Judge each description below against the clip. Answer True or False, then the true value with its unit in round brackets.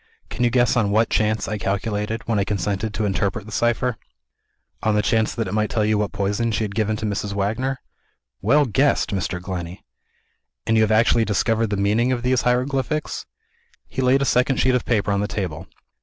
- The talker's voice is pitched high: False (110 Hz)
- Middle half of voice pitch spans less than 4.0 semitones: True (3.0 semitones)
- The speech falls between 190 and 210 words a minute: True (205 wpm)